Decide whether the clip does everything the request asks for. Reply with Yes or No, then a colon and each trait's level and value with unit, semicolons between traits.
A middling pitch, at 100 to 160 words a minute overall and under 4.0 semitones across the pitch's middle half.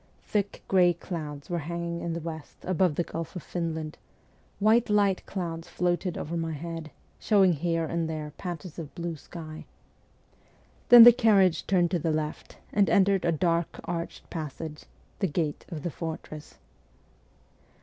Yes: medium, 170 Hz; average, 155 wpm; narrow, 2.4 semitones